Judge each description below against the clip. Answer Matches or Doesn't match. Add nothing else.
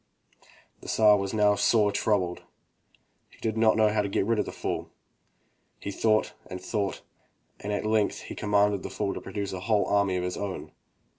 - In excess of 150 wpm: Matches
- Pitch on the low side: Matches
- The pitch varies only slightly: Matches